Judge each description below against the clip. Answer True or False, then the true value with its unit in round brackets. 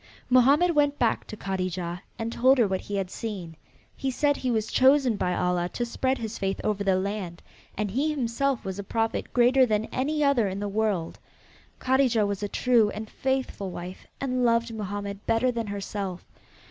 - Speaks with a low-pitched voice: False (220 Hz)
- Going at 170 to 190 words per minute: True (185 wpm)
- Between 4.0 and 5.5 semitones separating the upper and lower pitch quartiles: True (4.5 semitones)